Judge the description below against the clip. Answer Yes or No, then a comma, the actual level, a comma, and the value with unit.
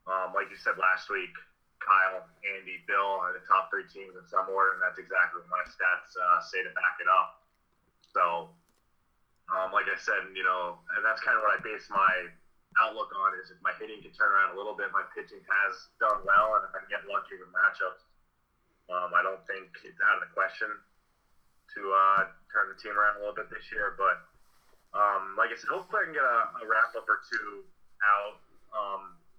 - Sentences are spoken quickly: Yes, fast, 215 wpm